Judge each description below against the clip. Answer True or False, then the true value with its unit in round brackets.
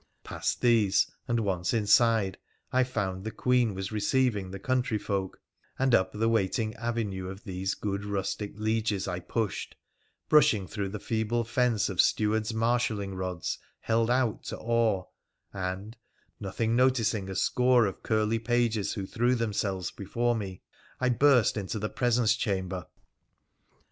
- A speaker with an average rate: True (145 wpm)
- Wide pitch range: False (3.3 semitones)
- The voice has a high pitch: False (110 Hz)